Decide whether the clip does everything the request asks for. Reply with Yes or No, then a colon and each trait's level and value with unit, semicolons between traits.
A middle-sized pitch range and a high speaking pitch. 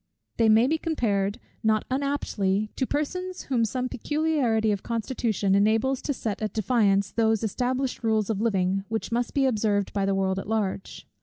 Yes: average, 4.1 semitones; high, 220 Hz